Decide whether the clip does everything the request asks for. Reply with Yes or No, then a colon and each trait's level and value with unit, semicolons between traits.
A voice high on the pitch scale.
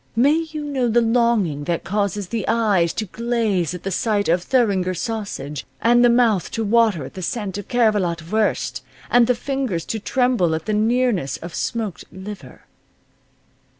Yes: high, 215 Hz